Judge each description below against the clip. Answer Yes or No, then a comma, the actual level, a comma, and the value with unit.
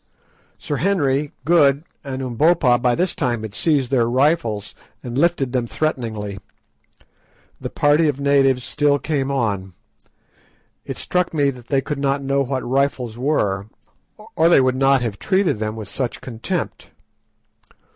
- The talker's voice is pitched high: No, low, 135 Hz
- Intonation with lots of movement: No, average, 3.5 semitones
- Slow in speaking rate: No, average, 145 wpm